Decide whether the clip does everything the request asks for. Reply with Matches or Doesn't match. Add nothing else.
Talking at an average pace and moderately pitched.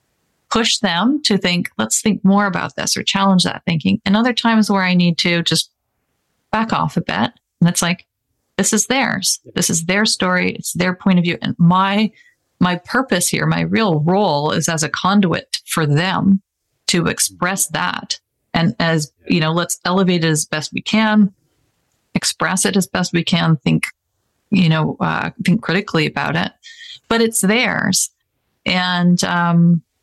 Matches